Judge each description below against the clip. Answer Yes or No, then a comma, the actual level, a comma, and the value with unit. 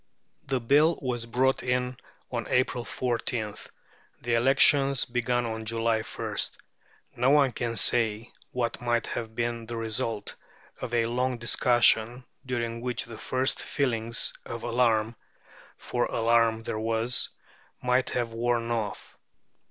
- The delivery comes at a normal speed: No, slow, 130 wpm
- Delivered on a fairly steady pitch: Yes, narrow, 1.6 semitones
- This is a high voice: No, low, 120 Hz